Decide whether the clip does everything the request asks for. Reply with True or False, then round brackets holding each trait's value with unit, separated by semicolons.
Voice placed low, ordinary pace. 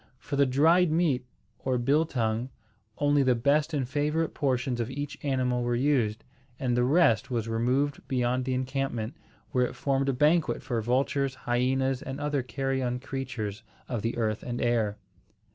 True (130 Hz; 160 wpm)